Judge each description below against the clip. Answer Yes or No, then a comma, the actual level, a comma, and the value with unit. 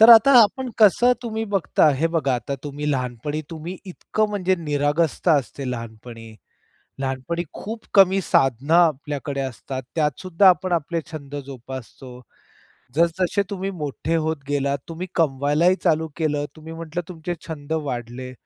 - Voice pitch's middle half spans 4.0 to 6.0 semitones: Yes, average, 4.7 semitones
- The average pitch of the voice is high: No, medium, 155 Hz